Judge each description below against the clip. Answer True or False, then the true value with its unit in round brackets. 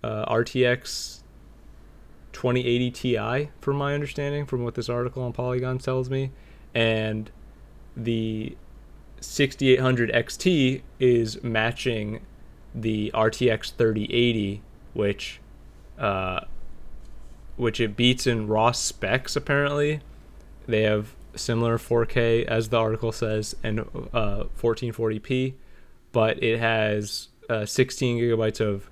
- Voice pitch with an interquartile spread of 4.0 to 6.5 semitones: False (2.9 semitones)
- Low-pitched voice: True (115 Hz)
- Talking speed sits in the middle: False (105 wpm)